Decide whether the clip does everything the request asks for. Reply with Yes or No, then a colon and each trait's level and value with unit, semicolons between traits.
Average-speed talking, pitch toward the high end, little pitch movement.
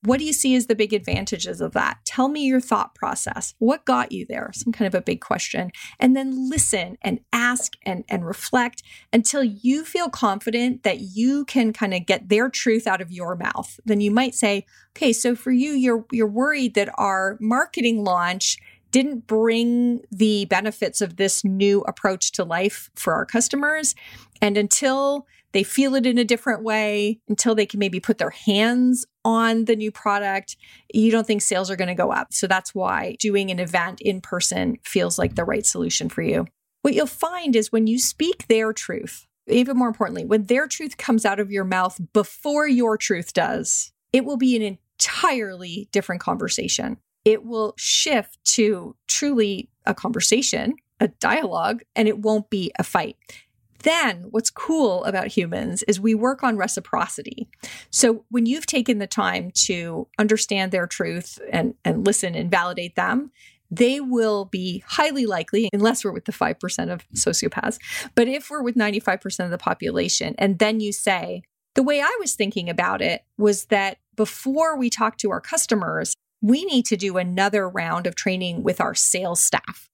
No: average, 180 wpm; high, 220 Hz; average, 4.0 semitones